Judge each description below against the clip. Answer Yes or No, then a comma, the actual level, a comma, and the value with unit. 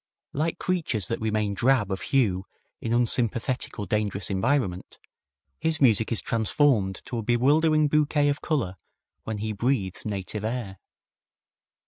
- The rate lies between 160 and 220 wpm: No, slow, 135 wpm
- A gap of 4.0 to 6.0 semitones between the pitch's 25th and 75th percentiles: Yes, average, 5.3 semitones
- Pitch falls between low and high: No, low, 115 Hz